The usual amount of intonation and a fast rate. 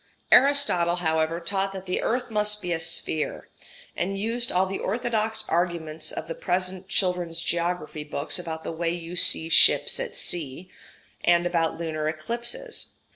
No: average, 3.9 semitones; average, 160 wpm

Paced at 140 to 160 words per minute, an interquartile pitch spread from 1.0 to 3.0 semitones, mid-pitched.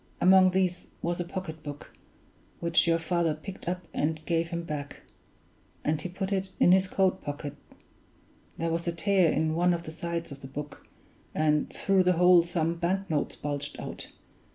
No: average, 175 wpm; narrow, 2.6 semitones; medium, 170 Hz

